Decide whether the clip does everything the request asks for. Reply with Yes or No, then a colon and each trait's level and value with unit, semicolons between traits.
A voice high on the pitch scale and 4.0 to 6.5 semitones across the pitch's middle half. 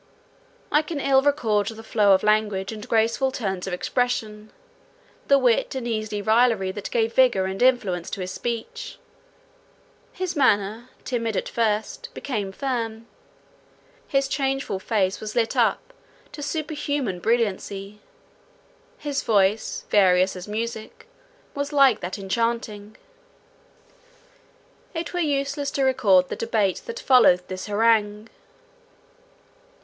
Yes: high, 225 Hz; average, 4.6 semitones